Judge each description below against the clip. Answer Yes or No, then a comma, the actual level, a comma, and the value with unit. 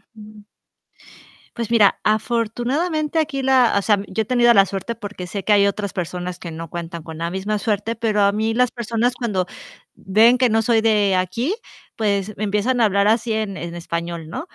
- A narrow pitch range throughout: No, average, 3.4 semitones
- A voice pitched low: No, high, 215 Hz